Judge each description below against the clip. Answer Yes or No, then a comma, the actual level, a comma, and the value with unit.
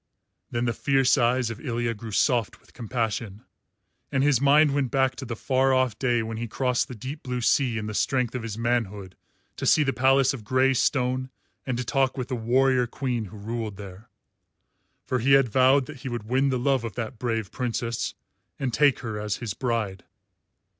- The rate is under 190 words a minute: No, average, 200 wpm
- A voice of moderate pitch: No, low, 125 Hz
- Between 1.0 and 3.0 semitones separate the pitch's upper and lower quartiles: Yes, average, 2.7 semitones